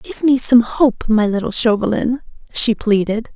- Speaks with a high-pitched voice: Yes, high, 230 Hz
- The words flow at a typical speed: Yes, average, 160 wpm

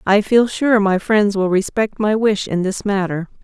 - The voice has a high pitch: Yes, high, 205 Hz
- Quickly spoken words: Yes, fast, 210 wpm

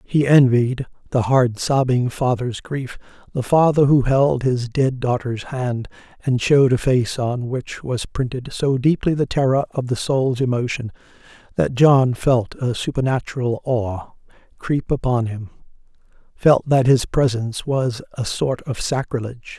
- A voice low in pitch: Yes, low, 125 Hz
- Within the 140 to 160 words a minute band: Yes, average, 150 wpm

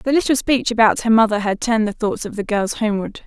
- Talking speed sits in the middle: No, fast, 260 wpm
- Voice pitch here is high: Yes, high, 220 Hz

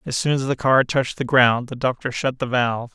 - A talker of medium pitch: No, low, 130 Hz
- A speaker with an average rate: No, fast, 265 wpm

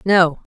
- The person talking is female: Yes, female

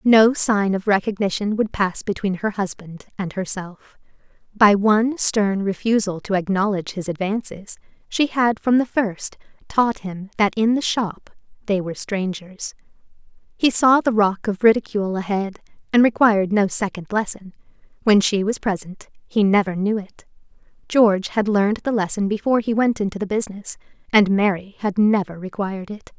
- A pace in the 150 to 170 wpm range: Yes, average, 160 wpm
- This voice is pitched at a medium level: No, high, 205 Hz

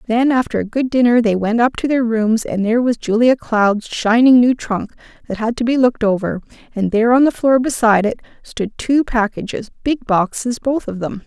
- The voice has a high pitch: Yes, high, 235 Hz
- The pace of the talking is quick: Yes, fast, 215 wpm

